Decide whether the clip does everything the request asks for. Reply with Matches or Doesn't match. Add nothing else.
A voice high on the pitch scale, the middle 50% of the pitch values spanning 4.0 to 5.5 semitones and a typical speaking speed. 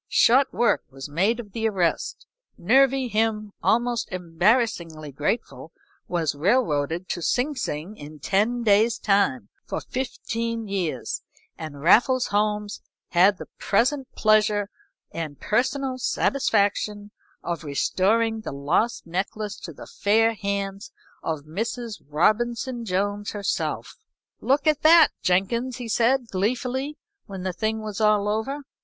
Doesn't match